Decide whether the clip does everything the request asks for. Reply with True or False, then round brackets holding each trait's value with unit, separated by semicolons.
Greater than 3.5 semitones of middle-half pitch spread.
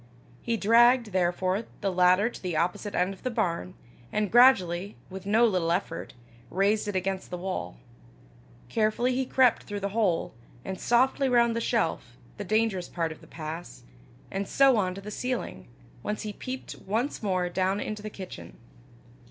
True (4.1 semitones)